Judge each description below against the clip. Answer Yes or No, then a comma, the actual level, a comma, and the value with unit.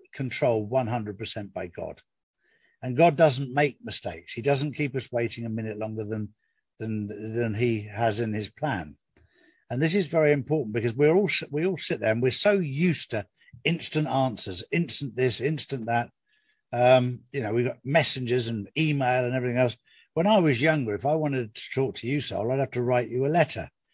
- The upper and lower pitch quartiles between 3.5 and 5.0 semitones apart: Yes, average, 4.6 semitones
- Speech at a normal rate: Yes, average, 195 wpm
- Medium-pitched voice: No, low, 130 Hz